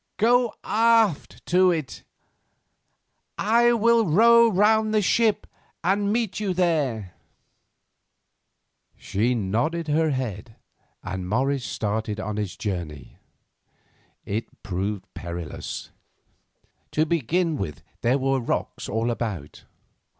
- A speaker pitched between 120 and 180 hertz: Yes, medium, 140 Hz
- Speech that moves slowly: Yes, slow, 105 wpm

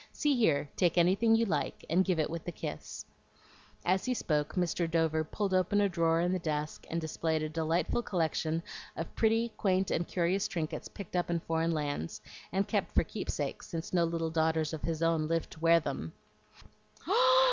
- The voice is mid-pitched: Yes, medium, 165 Hz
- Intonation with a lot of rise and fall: No, narrow, 2.6 semitones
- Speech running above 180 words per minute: Yes, average, 190 wpm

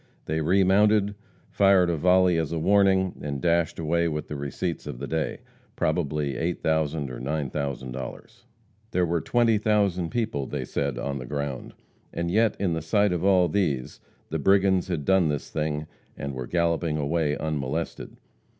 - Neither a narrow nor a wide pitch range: Yes, average, 4.4 semitones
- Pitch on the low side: Yes, very low, 80 Hz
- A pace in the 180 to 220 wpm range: No, average, 160 wpm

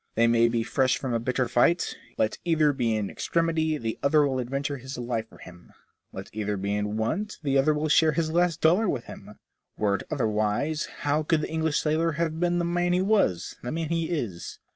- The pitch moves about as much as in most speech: No, wide, 5.7 semitones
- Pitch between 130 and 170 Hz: Yes, medium, 140 Hz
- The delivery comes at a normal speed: No, fast, 220 wpm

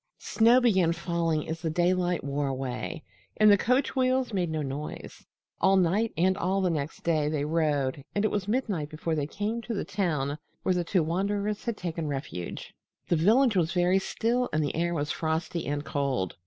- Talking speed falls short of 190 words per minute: No, average, 195 wpm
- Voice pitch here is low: No, medium, 170 Hz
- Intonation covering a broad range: No, average, 4.9 semitones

